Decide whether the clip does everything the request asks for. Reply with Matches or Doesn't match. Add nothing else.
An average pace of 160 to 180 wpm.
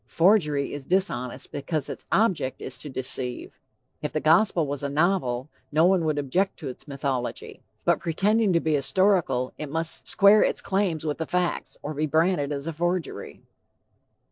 Matches